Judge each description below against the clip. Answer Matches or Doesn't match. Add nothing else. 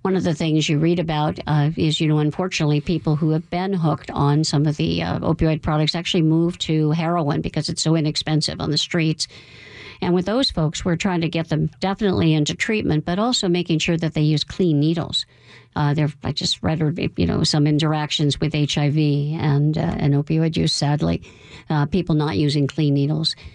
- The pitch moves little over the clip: Matches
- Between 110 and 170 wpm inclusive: Doesn't match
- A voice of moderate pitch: Matches